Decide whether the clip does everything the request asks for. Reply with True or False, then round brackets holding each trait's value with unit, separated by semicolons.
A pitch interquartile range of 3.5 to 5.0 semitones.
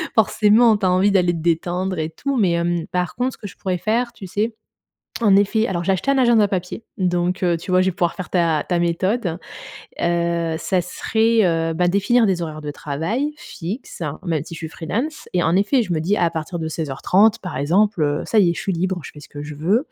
True (3.8 semitones)